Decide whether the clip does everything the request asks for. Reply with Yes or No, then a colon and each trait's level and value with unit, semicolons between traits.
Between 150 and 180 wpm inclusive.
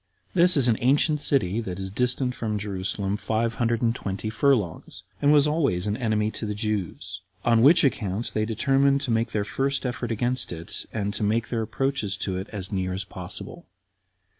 No: average, 190 wpm